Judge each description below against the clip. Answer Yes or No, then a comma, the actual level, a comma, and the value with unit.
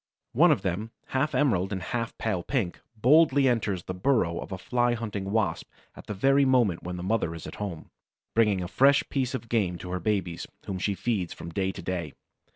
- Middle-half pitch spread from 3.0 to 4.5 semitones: No, average, 5.1 semitones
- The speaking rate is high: Yes, fast, 210 wpm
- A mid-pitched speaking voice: No, low, 105 Hz